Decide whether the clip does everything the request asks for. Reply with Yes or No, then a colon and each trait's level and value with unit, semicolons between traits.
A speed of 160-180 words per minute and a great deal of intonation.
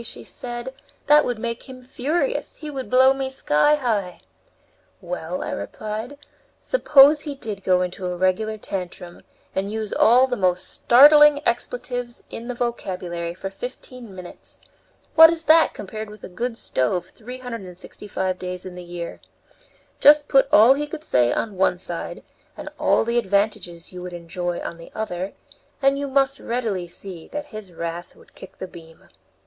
Yes: average, 165 wpm; wide, 6.4 semitones